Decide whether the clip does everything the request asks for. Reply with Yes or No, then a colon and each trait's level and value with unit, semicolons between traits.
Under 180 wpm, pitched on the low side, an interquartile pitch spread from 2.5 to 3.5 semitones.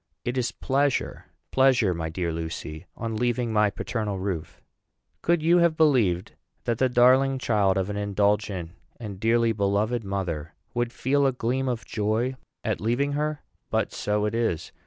No: average, 160 wpm; low, 115 Hz; average, 4.4 semitones